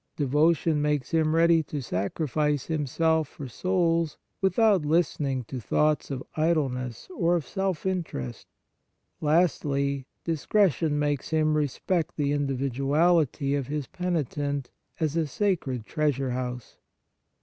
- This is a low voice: No, medium, 150 Hz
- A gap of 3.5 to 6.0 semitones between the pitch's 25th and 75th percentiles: No, average, 3.1 semitones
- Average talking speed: No, slow, 115 wpm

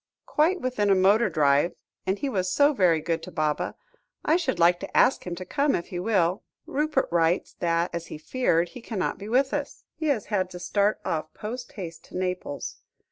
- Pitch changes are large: Yes, wide, 6.8 semitones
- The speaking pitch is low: No, medium, 185 Hz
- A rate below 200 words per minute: No, fast, 205 wpm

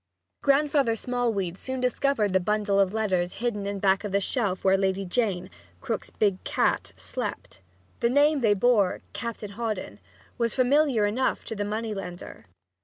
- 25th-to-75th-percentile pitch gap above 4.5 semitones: No, average, 3.9 semitones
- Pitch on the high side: Yes, high, 210 Hz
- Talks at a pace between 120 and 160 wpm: Yes, average, 155 wpm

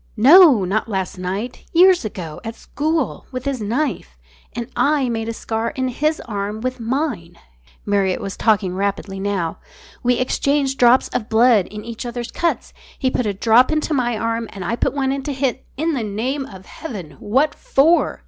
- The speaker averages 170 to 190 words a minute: Yes, average, 185 wpm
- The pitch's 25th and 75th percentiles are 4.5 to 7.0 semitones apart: Yes, average, 4.9 semitones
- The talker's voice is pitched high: Yes, high, 235 Hz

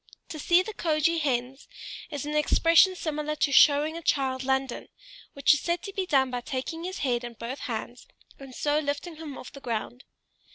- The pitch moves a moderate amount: Yes, average, 3.8 semitones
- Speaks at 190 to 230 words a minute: Yes, average, 195 wpm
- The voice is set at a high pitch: Yes, very high, 285 Hz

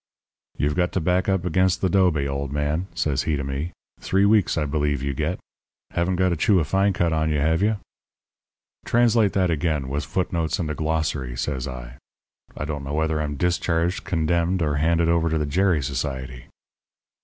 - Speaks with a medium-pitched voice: No, very low, 80 Hz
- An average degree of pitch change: Yes, average, 3.6 semitones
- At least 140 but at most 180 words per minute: No, average, 195 wpm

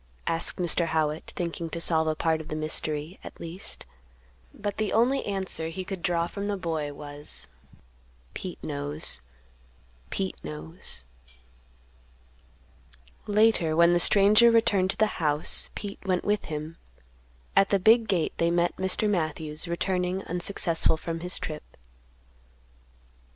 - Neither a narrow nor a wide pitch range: Yes, average, 3.7 semitones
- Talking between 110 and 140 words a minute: Yes, slow, 135 wpm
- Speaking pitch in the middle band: Yes, medium, 170 Hz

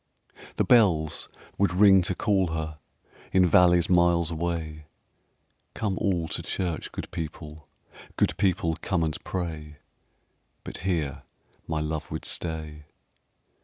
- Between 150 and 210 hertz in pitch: No, very low, 85 Hz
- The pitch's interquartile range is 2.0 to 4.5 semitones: Yes, average, 2.7 semitones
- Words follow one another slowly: Yes, slow, 125 wpm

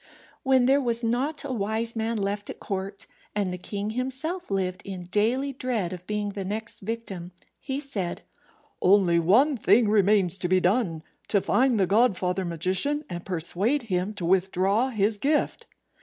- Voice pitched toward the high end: Yes, high, 205 Hz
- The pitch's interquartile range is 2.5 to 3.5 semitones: No, average, 4.8 semitones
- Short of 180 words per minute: Yes, average, 165 wpm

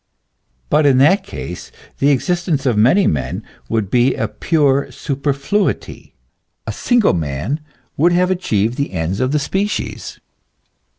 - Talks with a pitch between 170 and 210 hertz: No, medium, 140 Hz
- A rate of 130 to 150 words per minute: Yes, slow, 135 wpm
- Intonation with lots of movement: Yes, wide, 7.8 semitones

